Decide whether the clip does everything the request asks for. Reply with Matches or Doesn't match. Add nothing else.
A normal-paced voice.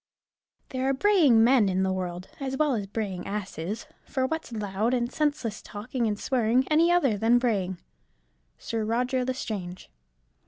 Matches